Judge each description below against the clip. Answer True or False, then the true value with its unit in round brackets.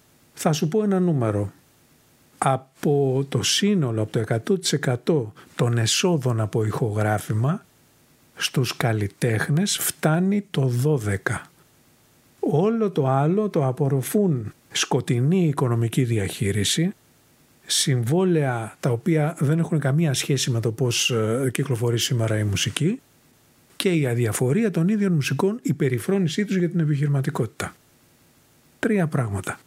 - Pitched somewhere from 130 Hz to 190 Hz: True (140 Hz)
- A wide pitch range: True (5.9 semitones)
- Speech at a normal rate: False (115 wpm)